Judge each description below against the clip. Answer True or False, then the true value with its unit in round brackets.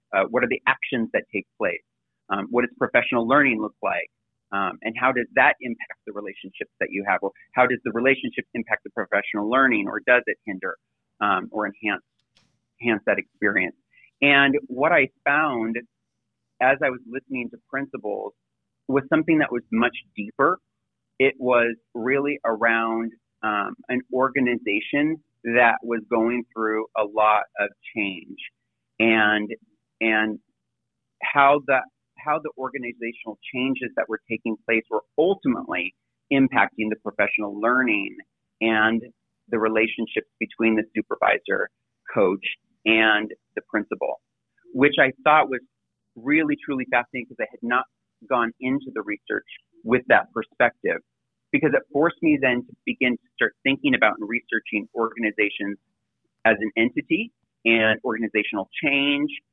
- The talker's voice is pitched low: True (120 Hz)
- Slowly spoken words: False (145 wpm)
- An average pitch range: True (3.7 semitones)